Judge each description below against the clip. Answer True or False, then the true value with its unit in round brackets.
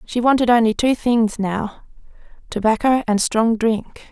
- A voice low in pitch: False (230 Hz)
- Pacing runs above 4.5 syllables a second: False (4.3 syllables/s)